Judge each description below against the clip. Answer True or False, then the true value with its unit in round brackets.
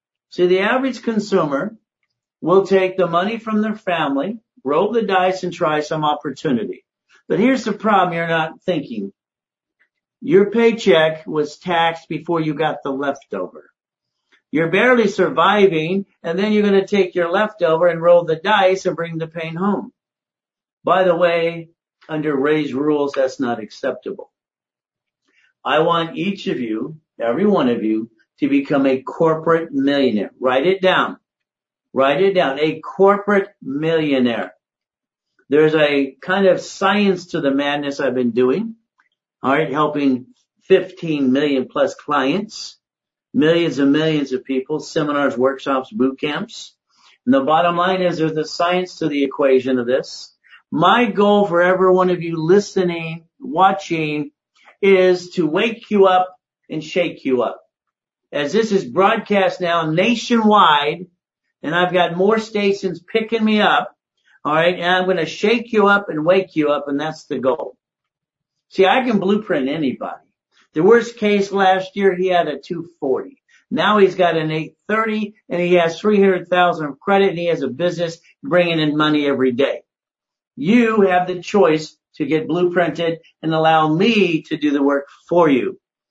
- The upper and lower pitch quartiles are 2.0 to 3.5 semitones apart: False (4.3 semitones)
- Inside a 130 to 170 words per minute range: True (155 wpm)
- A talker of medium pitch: True (175 Hz)